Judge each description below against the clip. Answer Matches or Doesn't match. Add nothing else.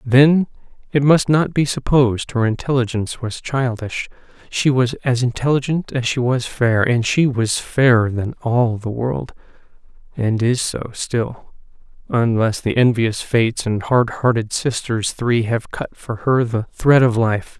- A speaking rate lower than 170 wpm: Matches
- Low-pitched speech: Matches